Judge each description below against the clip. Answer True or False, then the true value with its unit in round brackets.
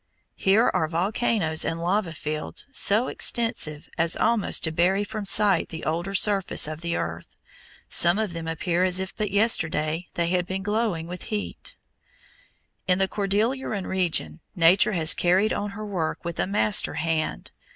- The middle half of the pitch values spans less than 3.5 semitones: False (4.0 semitones)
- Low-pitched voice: False (185 Hz)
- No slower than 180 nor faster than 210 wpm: False (160 wpm)